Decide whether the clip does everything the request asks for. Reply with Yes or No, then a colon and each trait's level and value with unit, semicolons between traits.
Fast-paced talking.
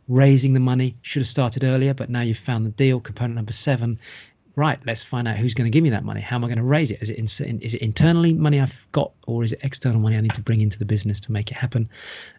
Yes: fast, 285 wpm